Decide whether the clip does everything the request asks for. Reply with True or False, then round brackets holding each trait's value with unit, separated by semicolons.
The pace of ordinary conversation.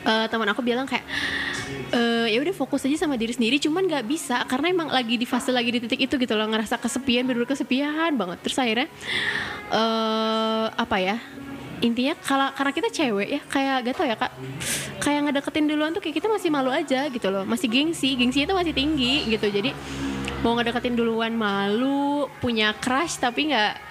False (190 wpm)